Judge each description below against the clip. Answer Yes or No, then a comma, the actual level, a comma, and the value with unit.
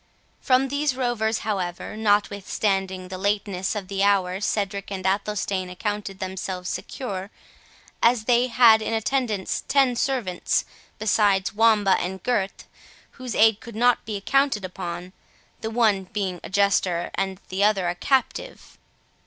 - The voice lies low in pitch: No, high, 205 Hz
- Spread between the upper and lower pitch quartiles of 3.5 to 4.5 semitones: No, average, 3.1 semitones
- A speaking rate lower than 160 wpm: Yes, slow, 135 wpm